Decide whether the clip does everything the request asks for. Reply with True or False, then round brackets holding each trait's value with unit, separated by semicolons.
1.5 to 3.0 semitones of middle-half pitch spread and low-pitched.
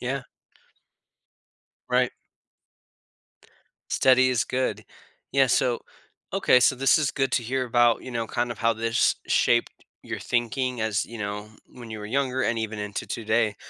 True (2.4 semitones; 120 Hz)